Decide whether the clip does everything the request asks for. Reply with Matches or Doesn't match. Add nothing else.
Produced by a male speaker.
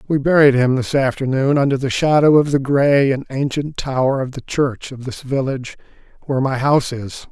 Matches